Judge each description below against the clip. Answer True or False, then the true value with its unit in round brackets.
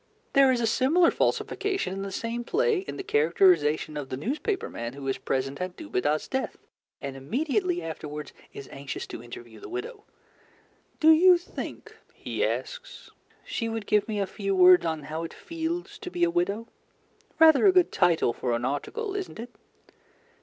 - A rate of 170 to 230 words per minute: True (175 wpm)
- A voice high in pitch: True (225 Hz)